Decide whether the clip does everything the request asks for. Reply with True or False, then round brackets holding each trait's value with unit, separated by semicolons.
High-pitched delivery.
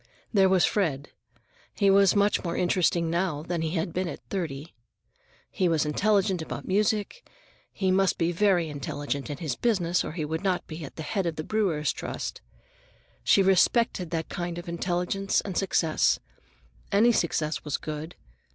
False (175 Hz)